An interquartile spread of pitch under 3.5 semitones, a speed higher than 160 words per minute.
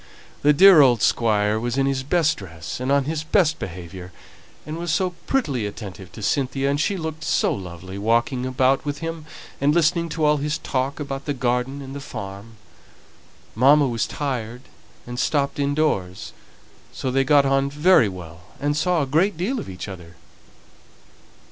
No: average, 5.0 semitones; average, 175 wpm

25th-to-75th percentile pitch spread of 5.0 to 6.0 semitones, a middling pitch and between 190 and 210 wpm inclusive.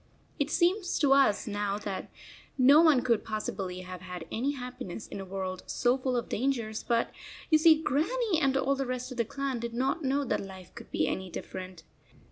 No: wide, 5.6 semitones; very high, 250 Hz; average, 200 wpm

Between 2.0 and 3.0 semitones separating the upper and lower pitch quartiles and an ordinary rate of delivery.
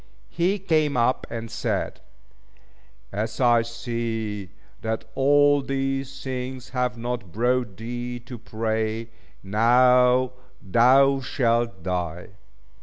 No: average, 2.7 semitones; slow, 105 wpm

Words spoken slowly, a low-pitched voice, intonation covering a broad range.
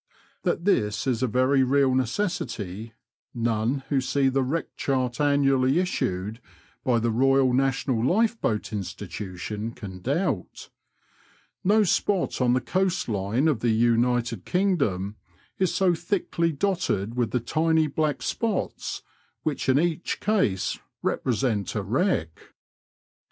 Yes: slow, 125 wpm; low, 130 Hz; wide, 6.1 semitones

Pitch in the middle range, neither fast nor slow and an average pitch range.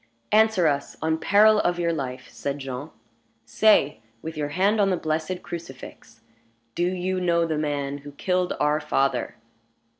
Yes: medium, 160 Hz; average, 155 wpm; average, 4.3 semitones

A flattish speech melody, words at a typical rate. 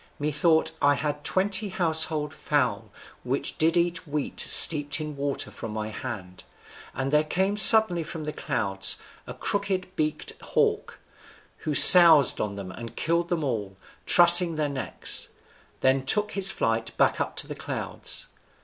No: average, 4.7 semitones; average, 150 wpm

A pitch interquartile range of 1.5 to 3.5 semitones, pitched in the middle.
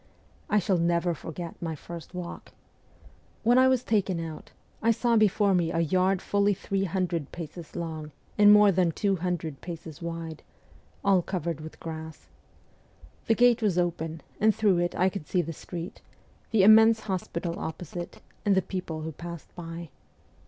Yes: average, 3.2 semitones; medium, 175 Hz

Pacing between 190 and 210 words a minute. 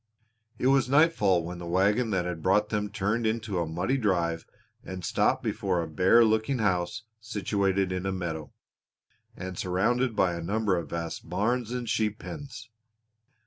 No: average, 165 wpm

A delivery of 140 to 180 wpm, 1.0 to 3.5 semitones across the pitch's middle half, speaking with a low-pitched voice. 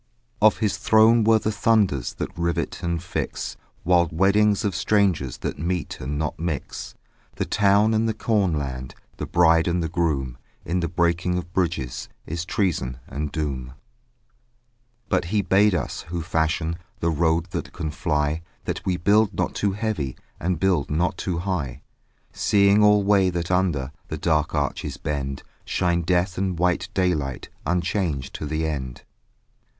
No: average, 155 wpm; average, 4.0 semitones; very low, 85 Hz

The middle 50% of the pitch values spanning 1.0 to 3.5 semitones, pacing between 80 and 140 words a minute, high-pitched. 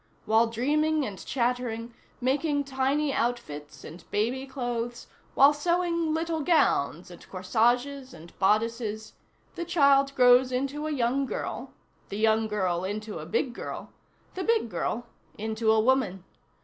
No: average, 4.4 semitones; slow, 135 wpm; high, 245 Hz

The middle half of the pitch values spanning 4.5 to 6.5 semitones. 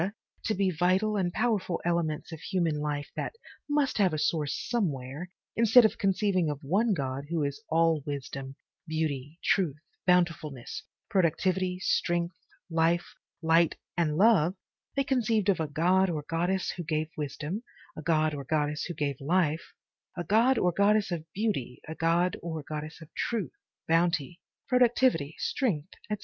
No: average, 4.0 semitones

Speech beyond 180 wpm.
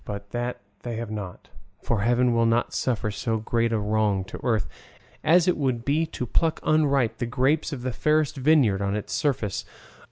Yes: average, 190 wpm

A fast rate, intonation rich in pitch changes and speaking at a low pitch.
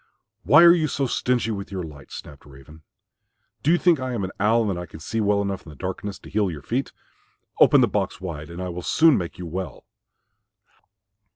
Yes: fast, 220 wpm; wide, 5.9 semitones; very low, 95 Hz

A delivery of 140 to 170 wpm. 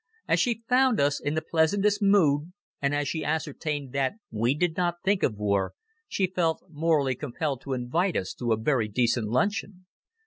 No: average, 180 wpm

